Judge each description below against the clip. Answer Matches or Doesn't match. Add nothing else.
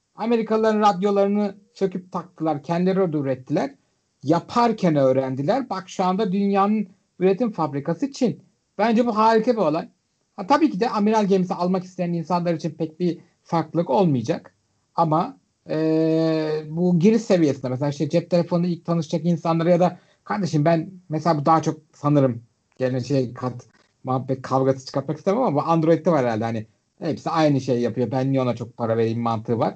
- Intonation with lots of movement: Matches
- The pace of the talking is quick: Matches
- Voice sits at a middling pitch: Matches